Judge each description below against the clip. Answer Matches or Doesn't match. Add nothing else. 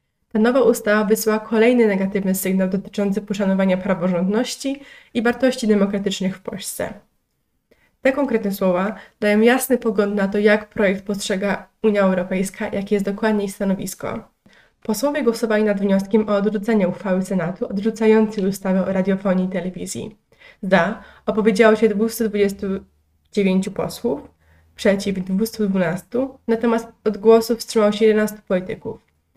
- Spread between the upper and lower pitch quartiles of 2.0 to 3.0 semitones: Matches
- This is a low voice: Doesn't match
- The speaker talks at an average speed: Matches